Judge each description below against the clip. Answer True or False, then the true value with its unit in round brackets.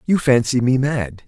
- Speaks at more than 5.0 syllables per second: False (4.4 syllables/s)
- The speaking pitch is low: True (130 Hz)